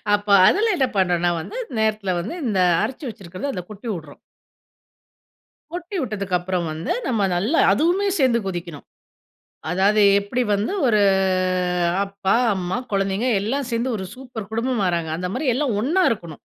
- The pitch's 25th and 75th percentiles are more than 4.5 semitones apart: Yes, wide, 5.4 semitones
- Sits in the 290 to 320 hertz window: No, high, 210 Hz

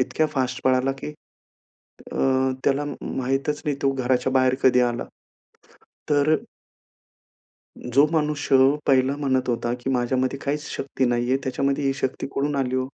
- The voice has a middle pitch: No, low, 130 Hz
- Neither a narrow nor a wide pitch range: No, narrow, 1.6 semitones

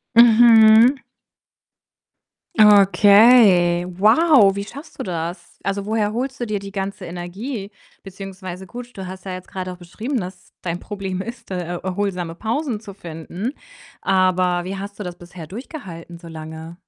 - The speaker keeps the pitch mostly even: No, average, 3.5 semitones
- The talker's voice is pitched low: No, high, 195 Hz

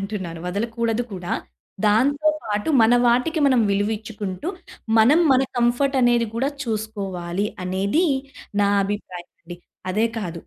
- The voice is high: Yes, high, 220 Hz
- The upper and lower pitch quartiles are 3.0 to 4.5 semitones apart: Yes, average, 3.8 semitones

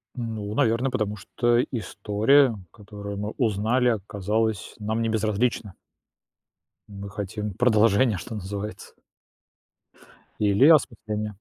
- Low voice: Yes, low, 105 Hz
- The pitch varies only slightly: Yes, narrow, 2.2 semitones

